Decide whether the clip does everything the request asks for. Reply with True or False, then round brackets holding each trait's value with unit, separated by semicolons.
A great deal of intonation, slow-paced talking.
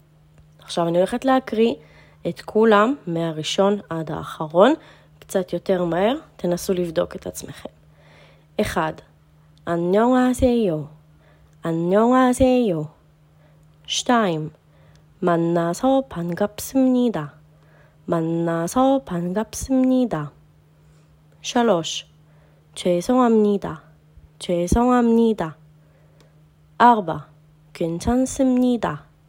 True (6.7 semitones; 65 wpm)